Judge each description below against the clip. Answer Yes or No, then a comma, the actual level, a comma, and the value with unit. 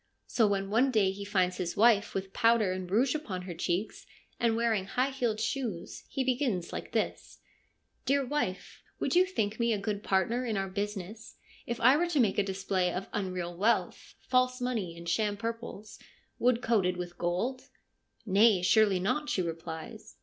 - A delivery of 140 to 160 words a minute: No, average, 185 wpm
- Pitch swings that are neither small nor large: Yes, average, 4.2 semitones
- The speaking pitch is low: No, high, 210 Hz